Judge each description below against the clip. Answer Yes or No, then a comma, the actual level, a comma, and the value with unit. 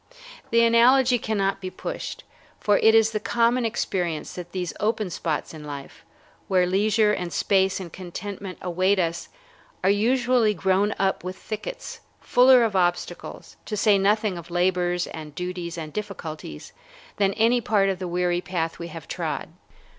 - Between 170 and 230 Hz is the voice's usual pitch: Yes, high, 190 Hz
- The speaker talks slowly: No, average, 160 wpm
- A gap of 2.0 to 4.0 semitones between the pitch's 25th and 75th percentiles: Yes, average, 3.6 semitones